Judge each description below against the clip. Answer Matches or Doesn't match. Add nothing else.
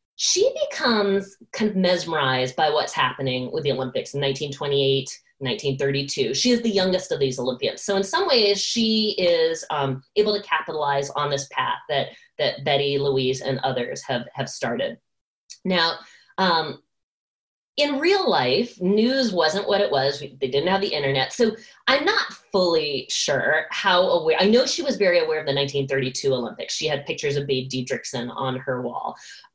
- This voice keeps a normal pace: Matches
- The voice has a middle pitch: Matches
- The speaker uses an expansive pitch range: Matches